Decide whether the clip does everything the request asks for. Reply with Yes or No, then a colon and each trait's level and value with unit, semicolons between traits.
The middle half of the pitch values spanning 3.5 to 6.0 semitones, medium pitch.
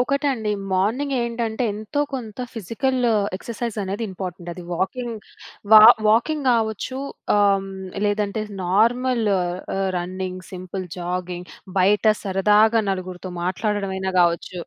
No: average, 3.9 semitones; high, 205 Hz